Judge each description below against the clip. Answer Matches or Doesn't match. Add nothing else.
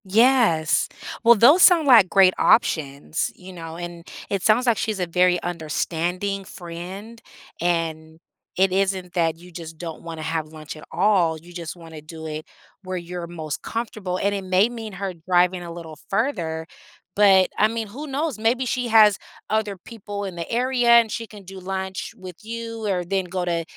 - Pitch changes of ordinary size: Matches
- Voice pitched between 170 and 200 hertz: Matches